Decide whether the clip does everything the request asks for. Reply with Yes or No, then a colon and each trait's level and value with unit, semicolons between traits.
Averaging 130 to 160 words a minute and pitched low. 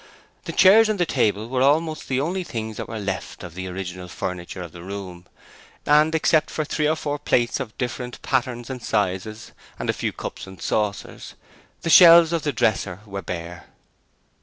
No: average, 185 wpm; low, 120 Hz